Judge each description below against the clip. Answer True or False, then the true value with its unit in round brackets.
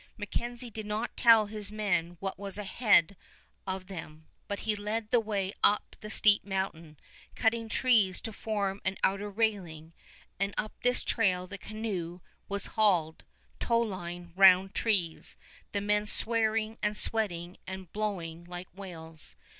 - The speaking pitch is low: False (200 Hz)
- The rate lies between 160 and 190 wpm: False (145 wpm)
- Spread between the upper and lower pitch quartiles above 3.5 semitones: False (3.1 semitones)